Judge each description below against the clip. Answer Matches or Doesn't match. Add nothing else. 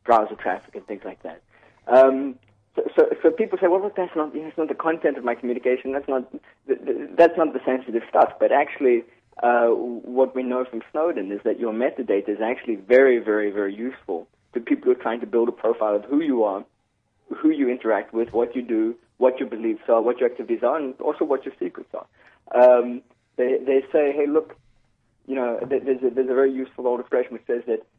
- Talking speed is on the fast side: Matches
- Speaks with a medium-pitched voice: Doesn't match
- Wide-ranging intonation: Matches